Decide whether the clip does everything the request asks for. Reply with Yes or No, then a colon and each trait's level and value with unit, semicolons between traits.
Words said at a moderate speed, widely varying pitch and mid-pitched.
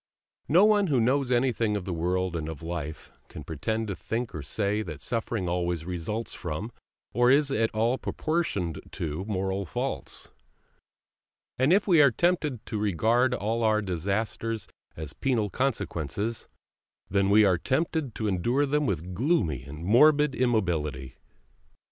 No: average, 150 wpm; wide, 6.3 semitones; low, 110 Hz